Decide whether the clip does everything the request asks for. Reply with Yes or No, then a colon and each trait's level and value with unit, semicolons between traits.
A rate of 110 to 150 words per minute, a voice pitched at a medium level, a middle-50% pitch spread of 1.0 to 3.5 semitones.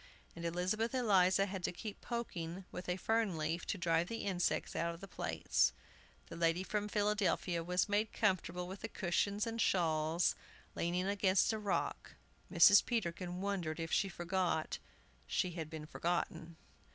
No: average, 160 wpm; medium, 180 Hz; average, 3.2 semitones